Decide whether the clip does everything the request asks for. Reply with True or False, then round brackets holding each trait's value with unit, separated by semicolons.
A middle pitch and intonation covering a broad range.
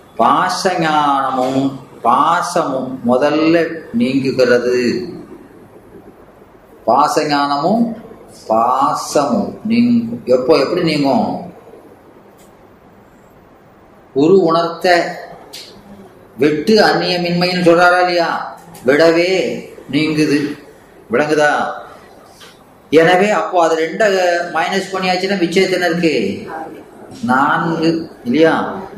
False (165 Hz; 3.7 semitones)